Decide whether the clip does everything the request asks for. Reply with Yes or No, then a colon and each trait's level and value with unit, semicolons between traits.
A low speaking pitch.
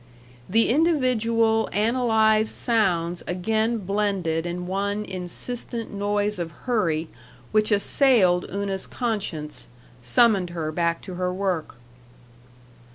No: high, 200 Hz